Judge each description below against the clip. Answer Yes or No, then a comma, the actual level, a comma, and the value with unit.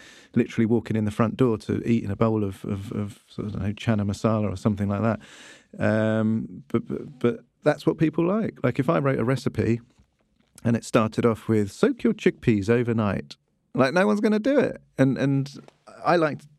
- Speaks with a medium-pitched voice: No, low, 115 Hz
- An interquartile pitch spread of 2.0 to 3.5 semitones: No, average, 4.1 semitones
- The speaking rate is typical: No, fast, 210 wpm